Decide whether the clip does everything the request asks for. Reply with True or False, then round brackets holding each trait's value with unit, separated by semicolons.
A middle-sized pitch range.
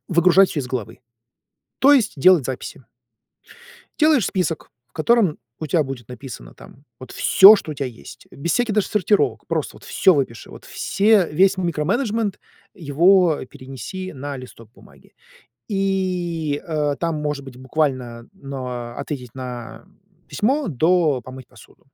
False (6.6 semitones)